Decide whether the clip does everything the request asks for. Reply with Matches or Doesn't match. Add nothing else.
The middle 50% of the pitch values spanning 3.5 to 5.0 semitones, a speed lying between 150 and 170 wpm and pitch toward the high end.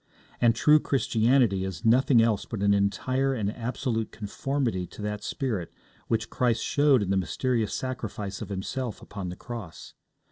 Doesn't match